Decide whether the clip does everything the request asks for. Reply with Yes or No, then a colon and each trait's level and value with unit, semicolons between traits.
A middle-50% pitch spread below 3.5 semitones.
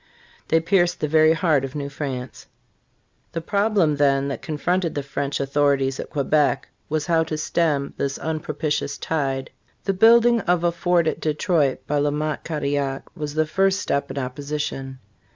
Yes: average, 3.0 semitones